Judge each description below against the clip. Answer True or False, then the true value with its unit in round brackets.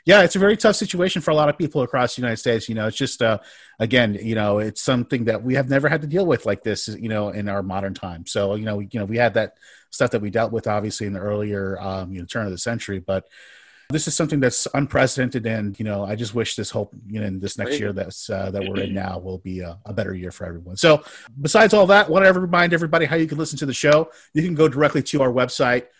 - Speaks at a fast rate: True (280 wpm)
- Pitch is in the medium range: False (115 Hz)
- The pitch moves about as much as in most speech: False (6.6 semitones)